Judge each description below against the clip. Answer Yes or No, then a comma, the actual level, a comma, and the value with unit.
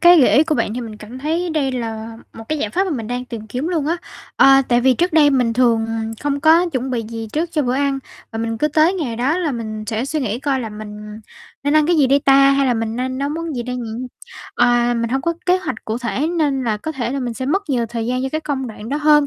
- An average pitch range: Yes, average, 4.5 semitones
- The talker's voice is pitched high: Yes, very high, 260 Hz